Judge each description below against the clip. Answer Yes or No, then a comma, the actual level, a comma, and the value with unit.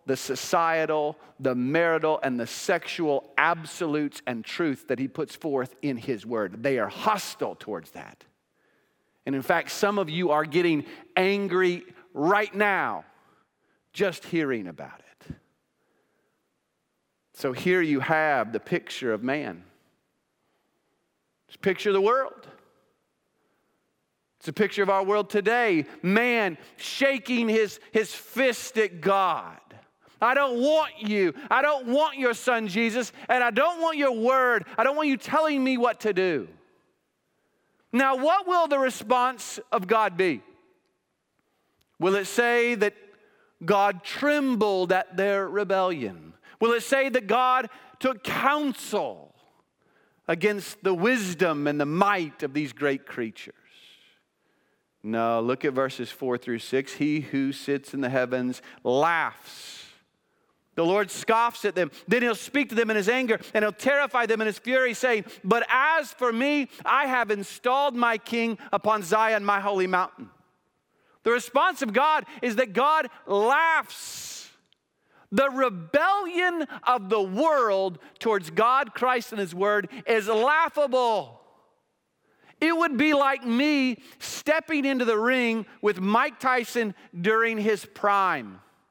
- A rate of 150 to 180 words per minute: No, average, 140 wpm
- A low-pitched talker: No, high, 220 Hz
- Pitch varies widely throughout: Yes, wide, 5.9 semitones